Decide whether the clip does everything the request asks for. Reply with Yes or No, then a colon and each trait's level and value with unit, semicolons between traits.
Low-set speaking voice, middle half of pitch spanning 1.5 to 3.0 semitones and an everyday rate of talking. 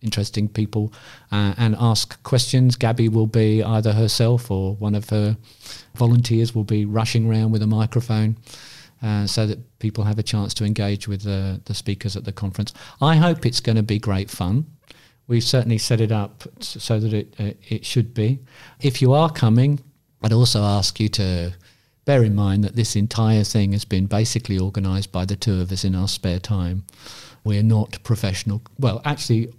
Yes: low, 110 Hz; narrow, 2.5 semitones; average, 190 wpm